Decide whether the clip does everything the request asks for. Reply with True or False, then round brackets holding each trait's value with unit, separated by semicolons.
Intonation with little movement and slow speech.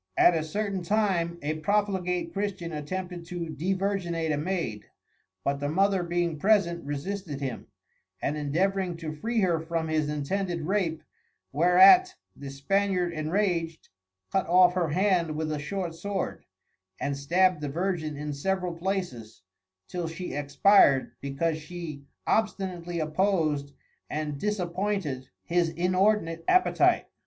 False (3.8 semitones; 130 wpm)